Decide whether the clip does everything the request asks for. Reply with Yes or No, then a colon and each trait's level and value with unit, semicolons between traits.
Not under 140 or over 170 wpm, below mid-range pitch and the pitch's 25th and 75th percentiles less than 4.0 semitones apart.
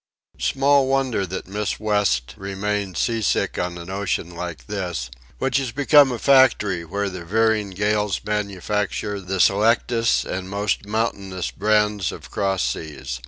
Yes: average, 145 wpm; low, 100 Hz; average, 3.1 semitones